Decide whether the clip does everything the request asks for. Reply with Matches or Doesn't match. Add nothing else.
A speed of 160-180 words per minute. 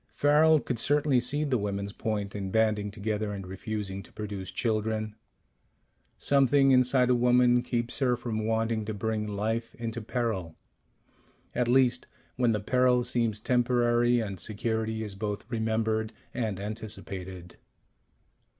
Doesn't match